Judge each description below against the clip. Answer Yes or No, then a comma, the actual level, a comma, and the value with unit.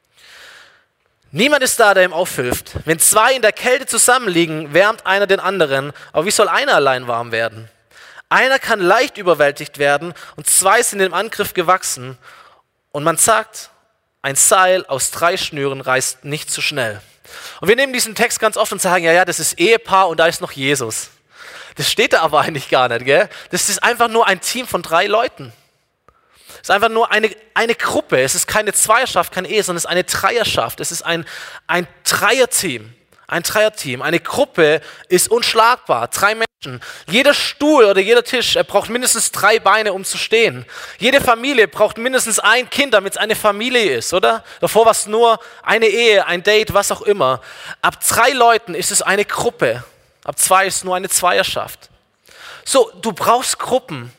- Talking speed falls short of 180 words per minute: No, average, 185 wpm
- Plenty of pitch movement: Yes, wide, 5.9 semitones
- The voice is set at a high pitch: Yes, high, 195 Hz